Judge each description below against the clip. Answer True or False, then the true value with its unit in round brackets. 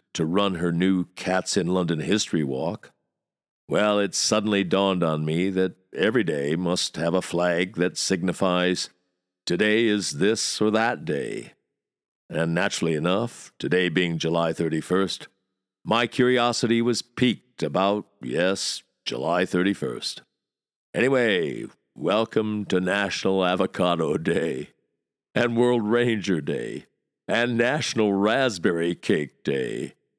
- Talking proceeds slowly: True (120 wpm)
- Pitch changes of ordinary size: True (3.2 semitones)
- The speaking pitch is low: True (95 Hz)